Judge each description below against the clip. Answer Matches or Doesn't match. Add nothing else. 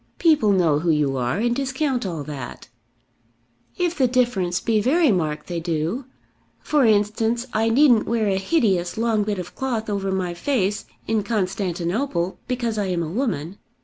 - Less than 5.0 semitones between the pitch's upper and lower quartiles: Doesn't match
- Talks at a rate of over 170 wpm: Doesn't match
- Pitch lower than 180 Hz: Doesn't match